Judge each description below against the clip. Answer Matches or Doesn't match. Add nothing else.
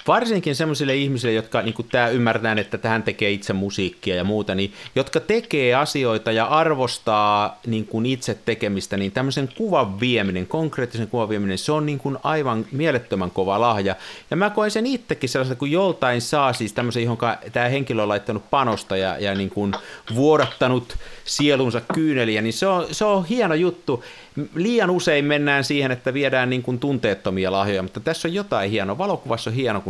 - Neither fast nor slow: Doesn't match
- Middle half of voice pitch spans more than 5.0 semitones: Matches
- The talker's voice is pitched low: Matches